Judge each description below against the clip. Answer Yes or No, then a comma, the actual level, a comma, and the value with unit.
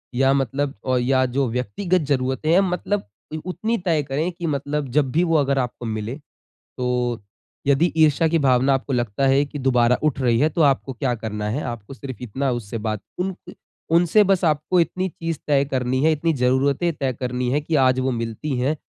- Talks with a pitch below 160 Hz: Yes, low, 135 Hz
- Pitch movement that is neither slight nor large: Yes, average, 3.8 semitones